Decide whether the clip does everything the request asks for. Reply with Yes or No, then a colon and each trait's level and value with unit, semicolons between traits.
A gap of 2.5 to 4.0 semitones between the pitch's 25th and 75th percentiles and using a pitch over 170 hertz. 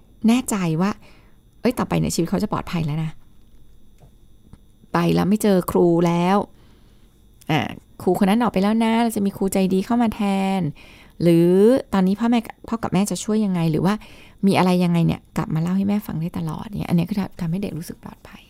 Yes: average, 3.7 semitones; high, 190 Hz